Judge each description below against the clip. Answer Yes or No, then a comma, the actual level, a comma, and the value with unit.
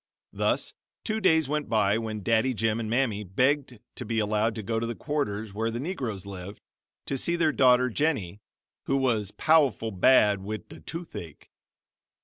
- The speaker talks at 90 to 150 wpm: No, average, 170 wpm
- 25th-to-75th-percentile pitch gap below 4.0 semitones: No, average, 4.5 semitones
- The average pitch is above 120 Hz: No, low, 115 Hz